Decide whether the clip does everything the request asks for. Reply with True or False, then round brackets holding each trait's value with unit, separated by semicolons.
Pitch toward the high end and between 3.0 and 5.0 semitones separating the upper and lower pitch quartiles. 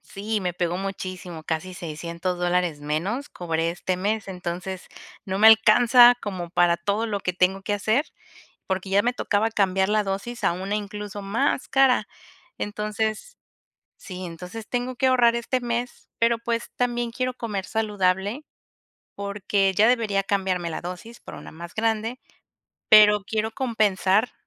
True (205 Hz; 3.7 semitones)